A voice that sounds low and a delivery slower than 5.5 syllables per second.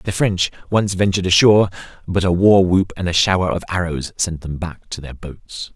Yes: very low, 90 Hz; 5.2 syllables/s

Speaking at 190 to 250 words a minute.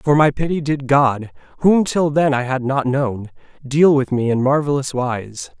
Yes: average, 195 wpm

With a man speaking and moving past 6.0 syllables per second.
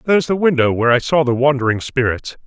Yes: male; 6.6 syllables/s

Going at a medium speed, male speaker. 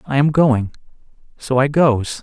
Yes: average, 160 wpm; male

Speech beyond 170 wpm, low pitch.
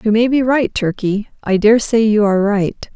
No: fast, 205 wpm; high, 215 Hz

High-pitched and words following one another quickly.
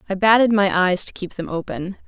Yes: high, 195 Hz; fast, 230 wpm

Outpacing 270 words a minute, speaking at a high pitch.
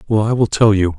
No: fast, 305 wpm; low, 105 Hz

